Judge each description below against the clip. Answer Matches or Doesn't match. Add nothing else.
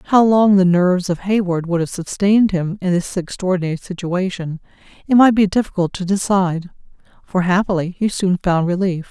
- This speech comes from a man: Doesn't match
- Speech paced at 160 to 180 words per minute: Matches